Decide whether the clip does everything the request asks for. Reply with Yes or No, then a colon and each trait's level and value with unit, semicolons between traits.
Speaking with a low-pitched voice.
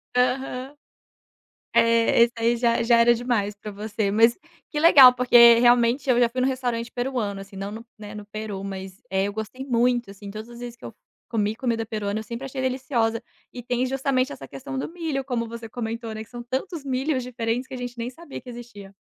No: high, 235 Hz